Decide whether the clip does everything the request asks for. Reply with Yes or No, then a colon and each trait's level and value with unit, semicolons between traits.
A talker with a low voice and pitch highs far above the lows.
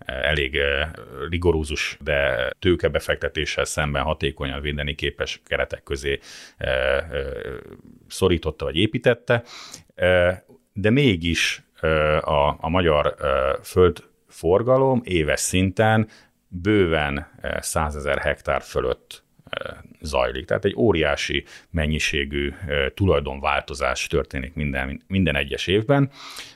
Yes: very low, 85 Hz; wide, 8.5 semitones